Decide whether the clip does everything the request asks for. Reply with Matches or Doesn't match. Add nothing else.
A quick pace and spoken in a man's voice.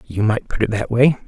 Matches